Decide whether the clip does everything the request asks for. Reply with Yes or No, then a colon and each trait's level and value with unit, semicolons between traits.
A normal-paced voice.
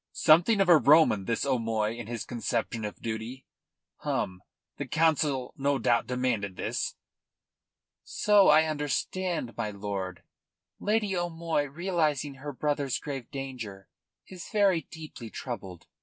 No: slow, 125 wpm